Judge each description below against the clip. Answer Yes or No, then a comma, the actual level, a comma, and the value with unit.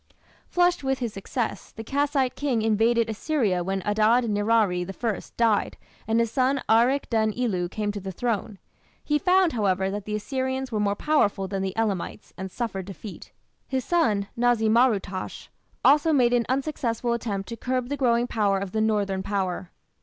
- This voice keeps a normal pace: Yes, average, 175 wpm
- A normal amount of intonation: Yes, average, 4.1 semitones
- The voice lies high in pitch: Yes, high, 225 Hz